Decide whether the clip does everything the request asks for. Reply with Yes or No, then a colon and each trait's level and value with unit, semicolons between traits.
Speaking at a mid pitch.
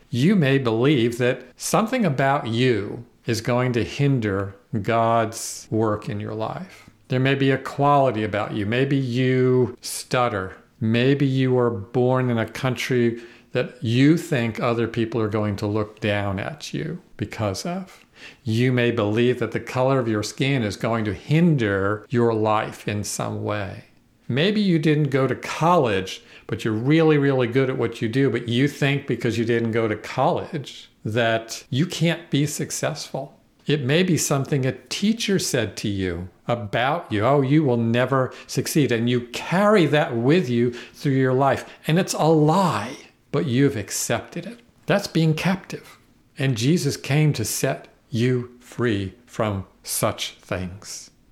No: low, 125 Hz